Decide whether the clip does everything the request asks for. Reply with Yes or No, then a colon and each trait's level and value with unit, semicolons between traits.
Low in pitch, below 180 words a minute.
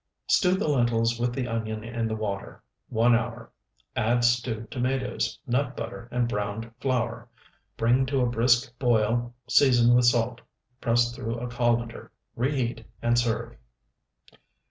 Yes: low, 120 Hz; average, 140 wpm